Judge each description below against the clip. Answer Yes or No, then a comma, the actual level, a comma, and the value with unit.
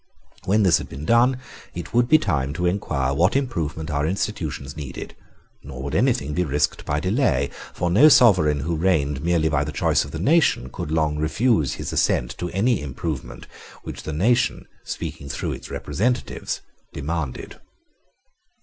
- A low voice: Yes, very low, 80 Hz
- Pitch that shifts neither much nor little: No, wide, 6.4 semitones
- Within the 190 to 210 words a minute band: No, average, 165 wpm